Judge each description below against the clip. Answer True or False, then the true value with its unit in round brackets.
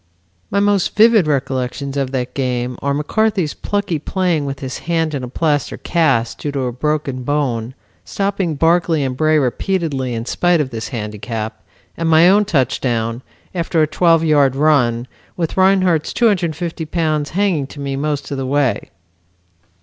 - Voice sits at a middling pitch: True (150 Hz)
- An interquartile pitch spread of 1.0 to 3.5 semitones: False (4.6 semitones)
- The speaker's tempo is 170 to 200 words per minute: False (160 wpm)